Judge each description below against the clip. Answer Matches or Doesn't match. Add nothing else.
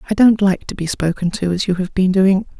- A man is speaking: Doesn't match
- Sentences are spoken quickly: Matches